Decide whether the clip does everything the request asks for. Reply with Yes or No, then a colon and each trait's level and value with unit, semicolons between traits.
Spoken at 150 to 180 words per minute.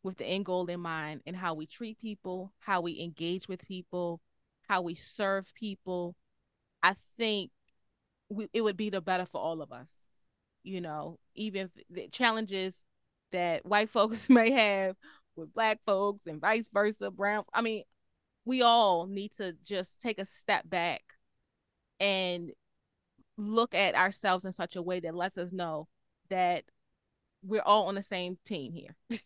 Yes: average, 165 wpm